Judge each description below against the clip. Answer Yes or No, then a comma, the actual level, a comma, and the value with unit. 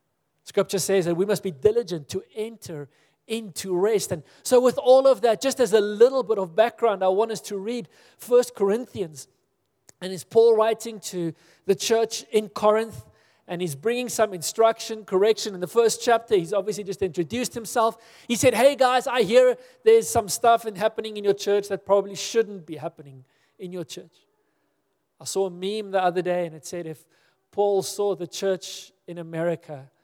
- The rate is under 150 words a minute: No, average, 185 wpm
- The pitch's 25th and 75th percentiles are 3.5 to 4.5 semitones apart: Yes, average, 4.0 semitones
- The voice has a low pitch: No, high, 205 Hz